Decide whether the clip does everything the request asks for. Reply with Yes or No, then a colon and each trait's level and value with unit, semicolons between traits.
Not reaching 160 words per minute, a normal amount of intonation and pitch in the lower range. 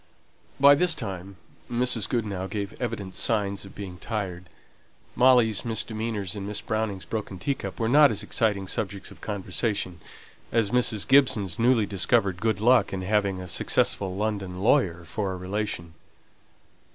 Yes: average, 145 wpm; average, 3.2 semitones; low, 105 Hz